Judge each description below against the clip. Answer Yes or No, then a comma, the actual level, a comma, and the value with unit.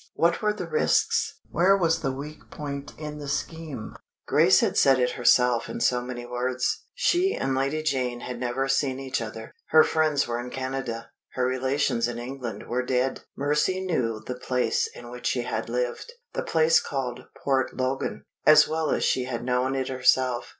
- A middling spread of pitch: Yes, average, 3.3 semitones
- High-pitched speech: No, low, 130 Hz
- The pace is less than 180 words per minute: No, average, 185 wpm